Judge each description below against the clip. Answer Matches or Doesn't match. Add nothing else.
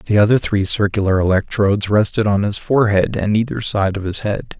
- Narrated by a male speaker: Matches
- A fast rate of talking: Doesn't match